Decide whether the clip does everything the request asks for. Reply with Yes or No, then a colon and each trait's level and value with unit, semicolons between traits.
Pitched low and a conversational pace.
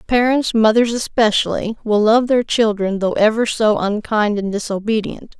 No: high, 220 Hz; average, 145 wpm